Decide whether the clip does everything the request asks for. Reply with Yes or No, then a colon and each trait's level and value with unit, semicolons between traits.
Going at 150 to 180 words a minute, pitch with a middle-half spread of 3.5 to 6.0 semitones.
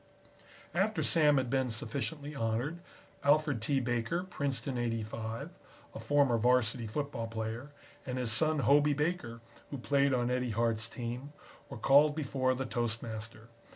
No: average, 140 wpm; average, 3.9 semitones